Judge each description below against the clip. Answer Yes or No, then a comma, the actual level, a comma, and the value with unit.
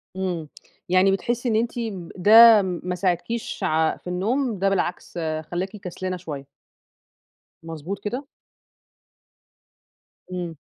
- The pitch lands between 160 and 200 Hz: Yes, medium, 185 Hz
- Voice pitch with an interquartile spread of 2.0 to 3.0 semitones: No, average, 3.7 semitones